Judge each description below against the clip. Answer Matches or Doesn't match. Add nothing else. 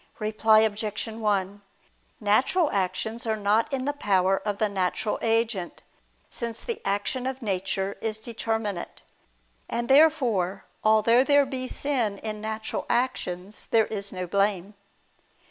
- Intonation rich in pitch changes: Doesn't match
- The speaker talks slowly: Matches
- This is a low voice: Doesn't match